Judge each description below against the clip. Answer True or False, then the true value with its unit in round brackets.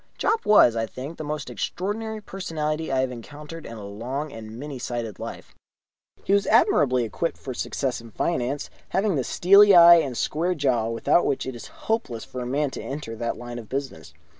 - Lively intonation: True (5.8 semitones)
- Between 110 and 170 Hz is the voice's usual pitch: True (135 Hz)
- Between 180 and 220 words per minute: True (195 wpm)